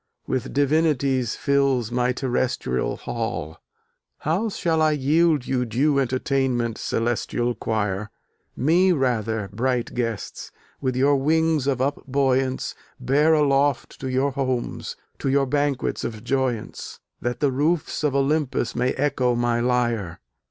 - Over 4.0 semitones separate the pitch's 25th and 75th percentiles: No, average, 2.9 semitones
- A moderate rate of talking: No, slow, 125 wpm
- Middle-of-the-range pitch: No, low, 130 Hz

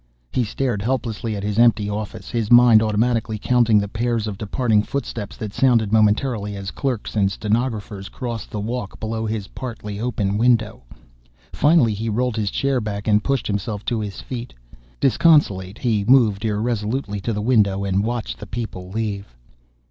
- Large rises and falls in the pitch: No, narrow, 2.6 semitones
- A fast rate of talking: No, average, 165 wpm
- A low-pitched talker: Yes, low, 110 Hz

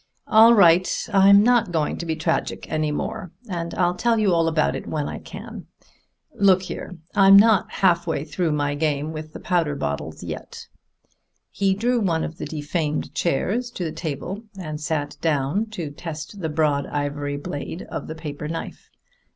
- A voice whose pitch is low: No, medium, 165 Hz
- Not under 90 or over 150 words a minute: No, average, 175 wpm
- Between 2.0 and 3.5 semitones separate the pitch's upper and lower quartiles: No, average, 4.3 semitones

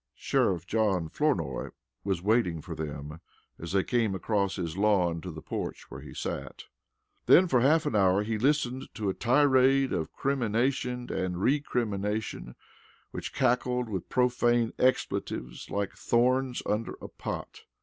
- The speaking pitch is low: Yes, low, 110 Hz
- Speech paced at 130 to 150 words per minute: Yes, average, 145 wpm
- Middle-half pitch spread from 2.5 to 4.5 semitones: No, average, 5.2 semitones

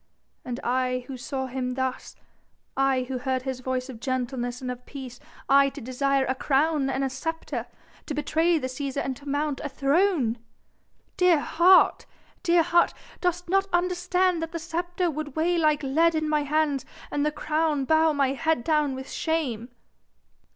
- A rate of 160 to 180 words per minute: Yes, average, 170 wpm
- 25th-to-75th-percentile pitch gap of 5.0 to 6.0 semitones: No, average, 3.8 semitones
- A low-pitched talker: No, very high, 285 Hz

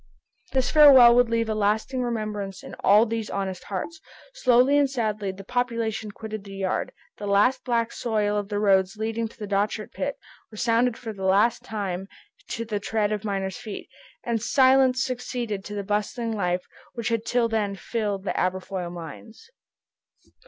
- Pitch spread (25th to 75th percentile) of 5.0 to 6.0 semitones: No, average, 3.0 semitones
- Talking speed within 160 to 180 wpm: Yes, average, 165 wpm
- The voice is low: No, high, 215 Hz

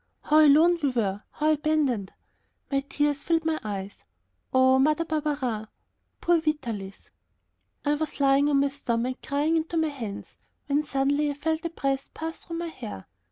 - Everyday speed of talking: Yes, average, 160 wpm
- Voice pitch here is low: No, very high, 285 Hz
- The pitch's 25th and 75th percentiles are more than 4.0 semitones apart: No, average, 3.2 semitones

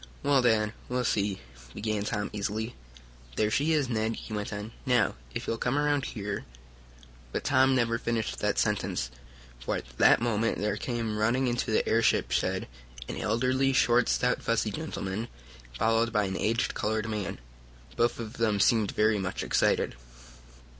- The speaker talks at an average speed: Yes, average, 160 wpm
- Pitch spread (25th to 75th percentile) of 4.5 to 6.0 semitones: No, narrow, 2.6 semitones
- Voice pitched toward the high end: No, low, 115 Hz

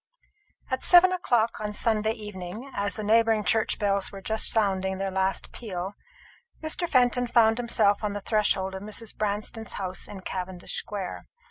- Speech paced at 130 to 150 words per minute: No, average, 160 wpm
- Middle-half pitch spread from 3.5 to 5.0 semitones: No, average, 2.8 semitones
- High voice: Yes, high, 210 Hz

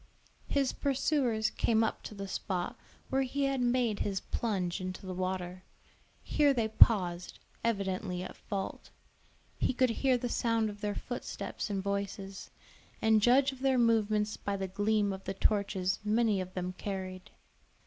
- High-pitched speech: Yes, high, 210 Hz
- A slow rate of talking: No, average, 160 wpm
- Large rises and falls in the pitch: No, average, 3.9 semitones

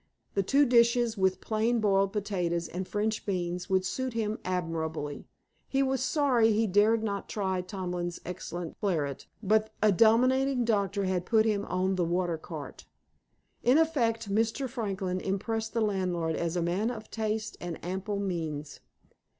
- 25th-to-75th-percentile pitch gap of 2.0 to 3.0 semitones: No, average, 3.9 semitones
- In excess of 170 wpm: No, average, 155 wpm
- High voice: Yes, high, 200 Hz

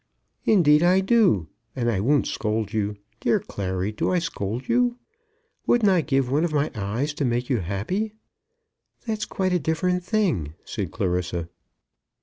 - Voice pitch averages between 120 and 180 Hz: Yes, medium, 140 Hz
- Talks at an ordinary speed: Yes, average, 155 wpm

